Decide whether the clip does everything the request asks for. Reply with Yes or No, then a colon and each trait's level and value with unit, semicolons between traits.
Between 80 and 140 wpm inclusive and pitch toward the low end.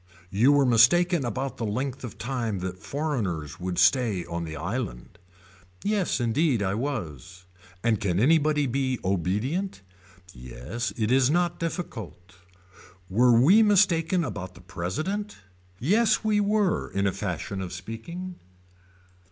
Yes: slow, 135 wpm; low, 120 Hz